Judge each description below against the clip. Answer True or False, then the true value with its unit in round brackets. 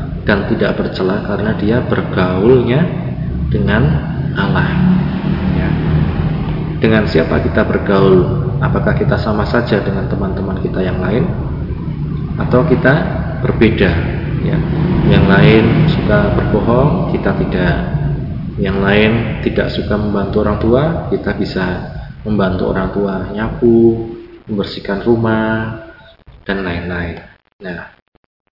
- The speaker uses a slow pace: False (105 wpm)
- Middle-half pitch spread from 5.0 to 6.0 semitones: True (5.5 semitones)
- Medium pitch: False (110 Hz)